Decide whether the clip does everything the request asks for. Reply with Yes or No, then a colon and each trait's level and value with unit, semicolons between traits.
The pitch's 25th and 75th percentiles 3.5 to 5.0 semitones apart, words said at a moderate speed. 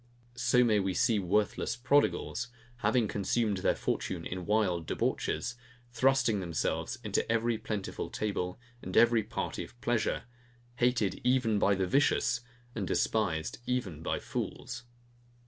No: average, 4.0 semitones; slow, 130 wpm